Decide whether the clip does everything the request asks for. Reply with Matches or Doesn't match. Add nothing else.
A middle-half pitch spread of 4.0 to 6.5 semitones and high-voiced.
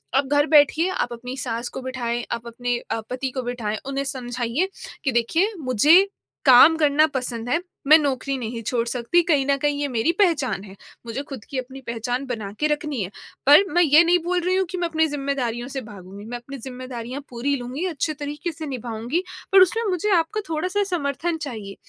Matches